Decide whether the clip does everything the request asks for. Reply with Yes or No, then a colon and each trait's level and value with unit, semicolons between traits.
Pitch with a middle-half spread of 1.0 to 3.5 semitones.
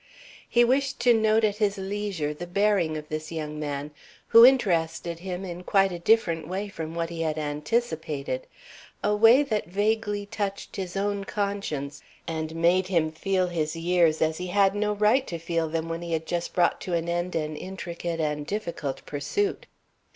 No: average, 4.2 semitones